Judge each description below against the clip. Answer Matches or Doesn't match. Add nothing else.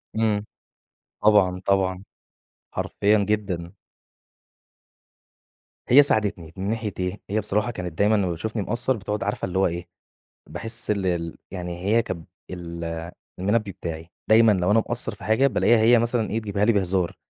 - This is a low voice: Matches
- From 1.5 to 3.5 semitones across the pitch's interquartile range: Matches